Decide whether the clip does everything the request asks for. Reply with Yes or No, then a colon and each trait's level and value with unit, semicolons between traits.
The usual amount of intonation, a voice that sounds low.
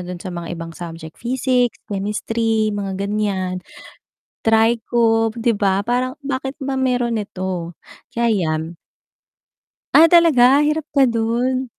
No: average, 4.8 semitones; high, 225 Hz